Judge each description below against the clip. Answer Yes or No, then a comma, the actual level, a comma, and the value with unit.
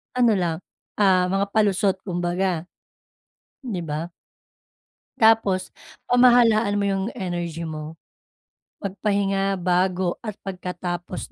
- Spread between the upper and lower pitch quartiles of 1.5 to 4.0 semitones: Yes, narrow, 2.5 semitones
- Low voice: No, high, 190 Hz